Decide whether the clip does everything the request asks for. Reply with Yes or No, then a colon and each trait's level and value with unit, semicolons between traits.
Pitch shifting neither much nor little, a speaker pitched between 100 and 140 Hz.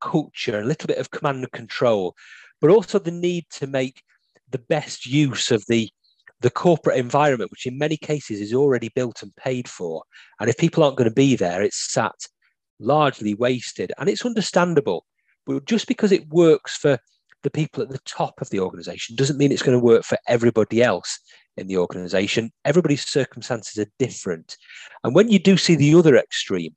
No: wide, 6.1 semitones; low, 135 Hz